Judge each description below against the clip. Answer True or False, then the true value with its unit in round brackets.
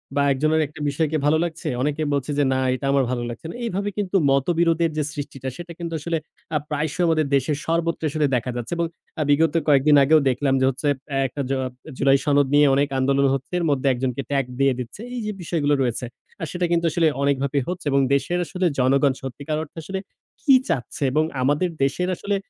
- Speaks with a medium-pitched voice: True (145 Hz)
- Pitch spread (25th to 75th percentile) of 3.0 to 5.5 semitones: True (3.5 semitones)